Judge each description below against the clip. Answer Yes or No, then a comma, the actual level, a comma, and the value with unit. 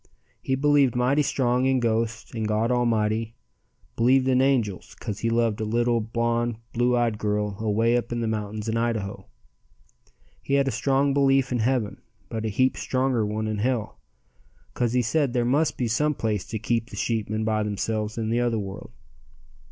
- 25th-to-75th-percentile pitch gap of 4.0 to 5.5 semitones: No, narrow, 2.6 semitones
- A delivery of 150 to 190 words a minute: Yes, average, 185 wpm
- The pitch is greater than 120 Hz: No, low, 115 Hz